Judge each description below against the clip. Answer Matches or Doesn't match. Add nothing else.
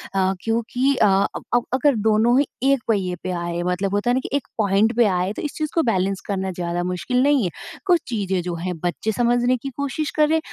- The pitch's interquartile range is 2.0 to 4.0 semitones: Doesn't match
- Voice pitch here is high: Matches